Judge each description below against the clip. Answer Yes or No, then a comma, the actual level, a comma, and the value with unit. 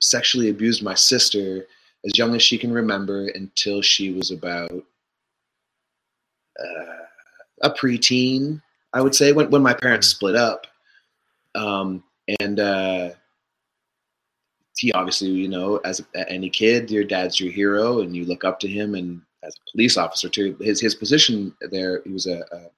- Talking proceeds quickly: No, average, 160 wpm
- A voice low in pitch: Yes, low, 100 Hz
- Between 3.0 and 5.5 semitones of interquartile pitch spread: Yes, average, 3.9 semitones